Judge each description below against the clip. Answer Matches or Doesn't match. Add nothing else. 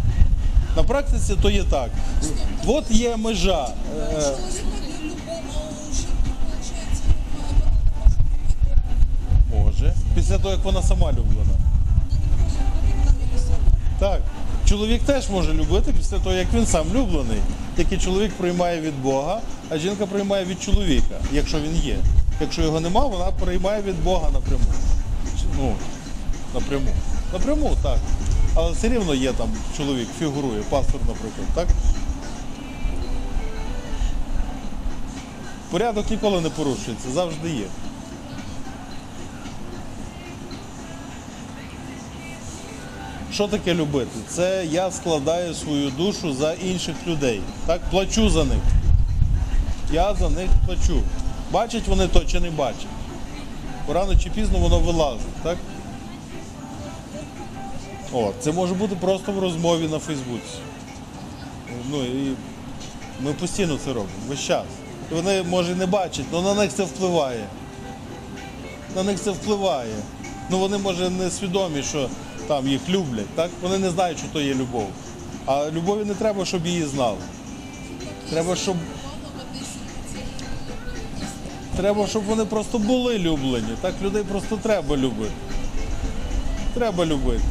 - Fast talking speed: Doesn't match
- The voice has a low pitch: Doesn't match